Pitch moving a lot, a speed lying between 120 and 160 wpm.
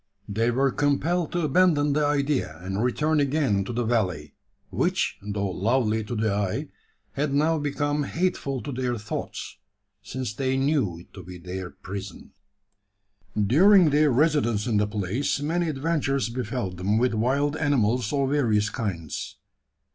Yes: wide, 5.9 semitones; average, 150 wpm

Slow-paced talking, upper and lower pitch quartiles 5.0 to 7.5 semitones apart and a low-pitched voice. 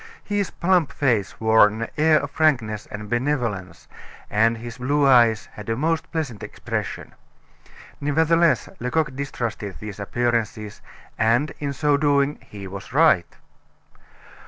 Yes: slow, 130 wpm; wide, 5.4 semitones; low, 125 Hz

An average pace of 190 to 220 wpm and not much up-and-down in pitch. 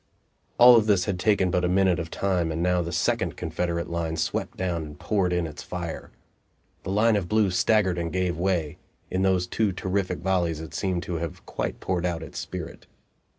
Yes: average, 195 wpm; narrow, 2.1 semitones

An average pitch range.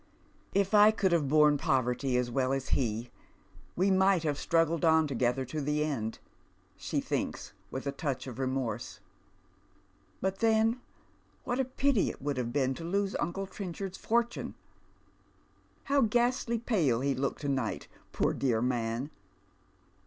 No: wide, 7.0 semitones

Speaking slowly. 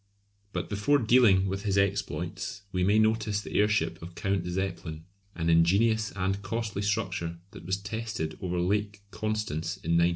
No: average, 160 wpm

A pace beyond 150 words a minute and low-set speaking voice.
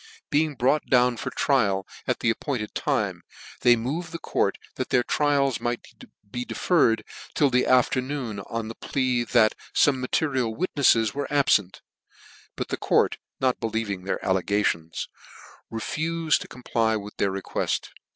No: average, 145 wpm; low, 125 Hz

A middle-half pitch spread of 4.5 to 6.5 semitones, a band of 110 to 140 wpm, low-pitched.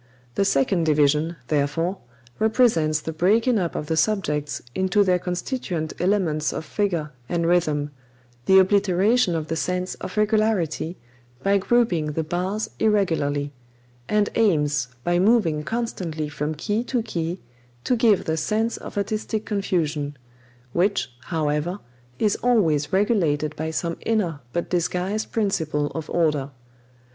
No: average, 5.1 semitones; slow, 135 wpm; medium, 175 Hz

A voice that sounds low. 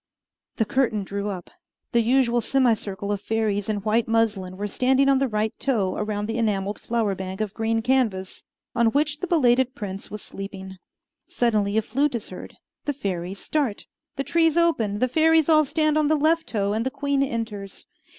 No: high, 225 Hz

